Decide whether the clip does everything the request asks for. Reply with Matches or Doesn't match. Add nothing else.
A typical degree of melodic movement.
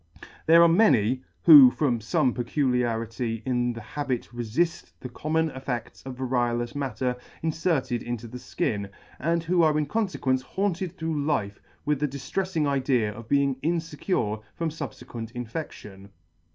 Matches